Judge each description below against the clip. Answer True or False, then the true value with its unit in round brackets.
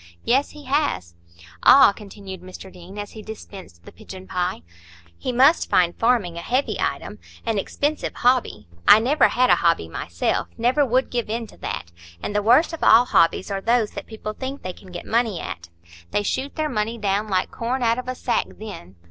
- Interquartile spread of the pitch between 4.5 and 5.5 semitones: True (5.1 semitones)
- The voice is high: True (220 Hz)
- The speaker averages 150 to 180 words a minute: False (190 wpm)